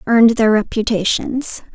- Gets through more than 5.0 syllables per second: No, 4.6 syllables/s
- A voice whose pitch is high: Yes, high, 225 Hz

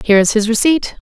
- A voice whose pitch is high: Yes, high, 230 Hz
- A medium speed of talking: No, fast, 225 wpm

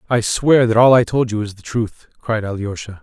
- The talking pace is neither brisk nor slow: No, fast, 240 wpm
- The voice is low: Yes, low, 110 Hz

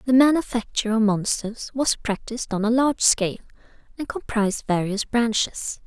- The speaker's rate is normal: Yes, average, 145 wpm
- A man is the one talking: No, female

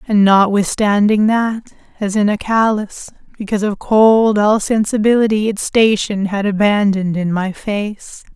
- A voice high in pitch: Yes, high, 210 Hz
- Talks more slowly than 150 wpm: Yes, slow, 135 wpm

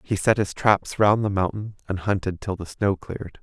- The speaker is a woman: No, male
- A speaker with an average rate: No, fast, 225 wpm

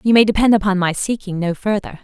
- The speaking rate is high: Yes, fast, 235 wpm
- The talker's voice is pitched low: No, high, 200 Hz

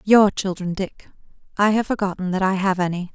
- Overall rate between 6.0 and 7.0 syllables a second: No, 5.4 syllables/s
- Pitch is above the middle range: Yes, high, 195 Hz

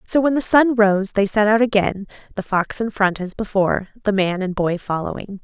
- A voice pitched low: No, high, 205 Hz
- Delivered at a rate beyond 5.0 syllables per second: Yes, 5.2 syllables/s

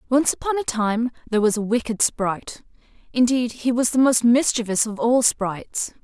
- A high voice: Yes, high, 235 Hz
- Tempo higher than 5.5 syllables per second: No, 5.1 syllables/s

